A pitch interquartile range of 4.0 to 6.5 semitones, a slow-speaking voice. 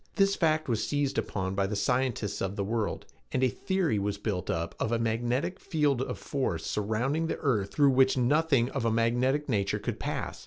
No: average, 5.3 semitones; average, 200 wpm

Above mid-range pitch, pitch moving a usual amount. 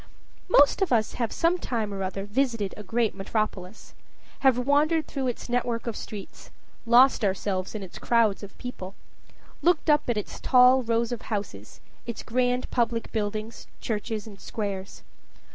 Yes: high, 230 Hz; average, 3.4 semitones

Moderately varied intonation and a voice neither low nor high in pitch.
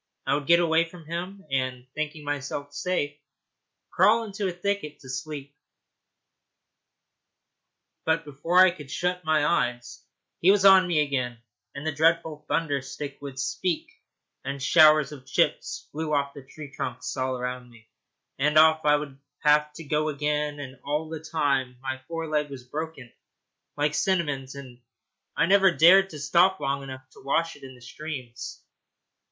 Yes: average, 3.2 semitones; medium, 150 Hz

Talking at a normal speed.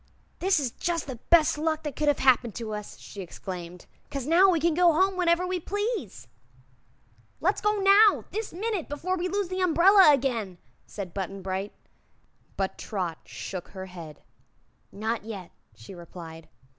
Yes: average, 165 wpm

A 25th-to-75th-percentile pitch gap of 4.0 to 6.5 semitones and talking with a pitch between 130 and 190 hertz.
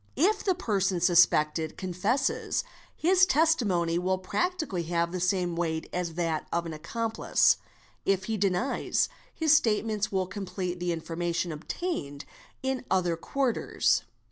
Yes: average, 5.1 semitones; medium, 185 Hz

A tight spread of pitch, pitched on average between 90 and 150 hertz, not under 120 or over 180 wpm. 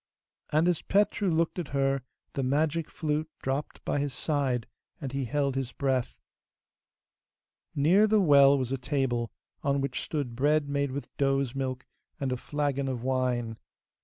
Yes: narrow, 2.3 semitones; medium, 140 Hz; average, 160 wpm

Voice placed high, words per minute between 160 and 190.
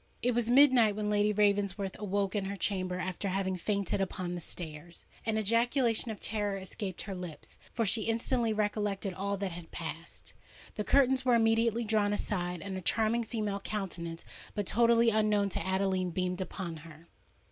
Yes: high, 200 Hz; average, 170 wpm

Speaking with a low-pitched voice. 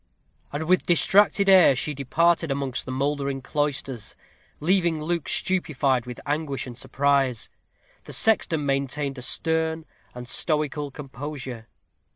No: medium, 145 Hz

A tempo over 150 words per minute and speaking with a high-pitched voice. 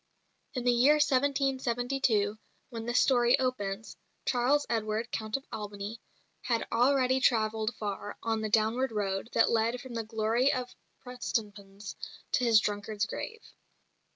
No: slow, 135 wpm; high, 230 Hz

